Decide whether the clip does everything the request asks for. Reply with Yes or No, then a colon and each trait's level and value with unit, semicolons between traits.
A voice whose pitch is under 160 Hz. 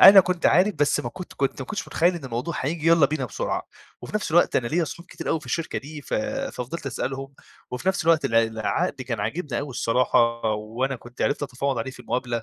Yes: medium, 140 Hz